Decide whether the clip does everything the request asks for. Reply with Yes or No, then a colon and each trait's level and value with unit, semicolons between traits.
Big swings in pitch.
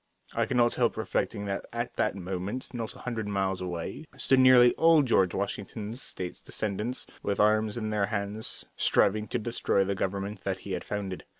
No: average, 3.3 semitones